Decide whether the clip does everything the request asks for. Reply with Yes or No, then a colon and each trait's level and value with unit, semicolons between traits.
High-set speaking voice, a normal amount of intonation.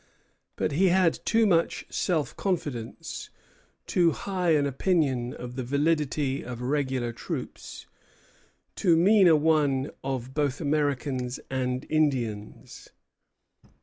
No: medium, 145 Hz; average, 4.3 semitones